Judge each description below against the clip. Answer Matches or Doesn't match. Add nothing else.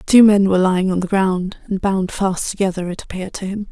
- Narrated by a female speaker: Matches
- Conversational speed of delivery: Doesn't match